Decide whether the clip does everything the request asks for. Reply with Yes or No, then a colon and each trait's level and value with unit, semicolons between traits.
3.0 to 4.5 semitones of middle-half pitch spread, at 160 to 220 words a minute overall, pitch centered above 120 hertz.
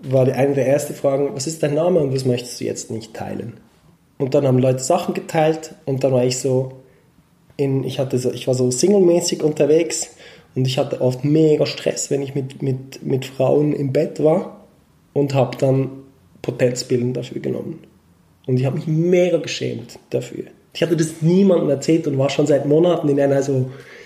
Yes: average, 3.3 semitones; fast, 190 wpm; medium, 140 Hz